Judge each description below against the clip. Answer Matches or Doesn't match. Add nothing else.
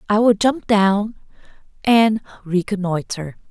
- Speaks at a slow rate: Matches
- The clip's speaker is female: Matches